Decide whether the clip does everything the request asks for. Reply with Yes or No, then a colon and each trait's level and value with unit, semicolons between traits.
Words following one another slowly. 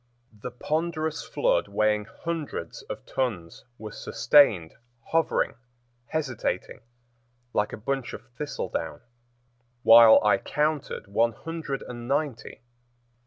Yes: slow, 105 wpm